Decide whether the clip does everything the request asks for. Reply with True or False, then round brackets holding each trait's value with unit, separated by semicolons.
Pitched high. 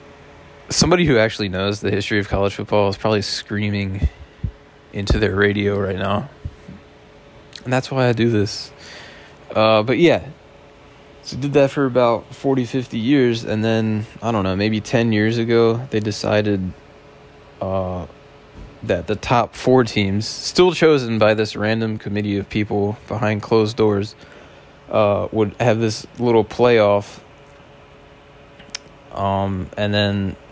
False (110 Hz)